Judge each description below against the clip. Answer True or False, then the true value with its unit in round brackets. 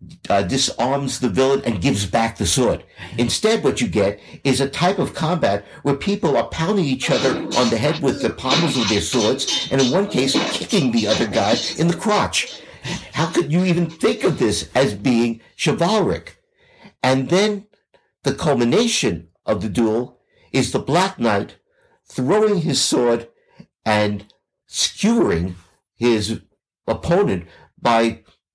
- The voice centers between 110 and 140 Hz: True (135 Hz)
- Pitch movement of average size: False (7.7 semitones)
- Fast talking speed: False (155 wpm)